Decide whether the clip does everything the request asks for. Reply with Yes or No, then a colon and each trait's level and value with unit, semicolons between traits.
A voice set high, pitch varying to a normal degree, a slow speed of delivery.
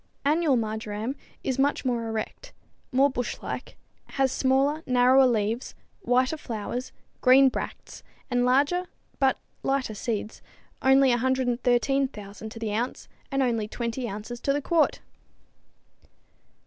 Yes: very high, 255 Hz; average, 3.0 semitones; slow, 120 wpm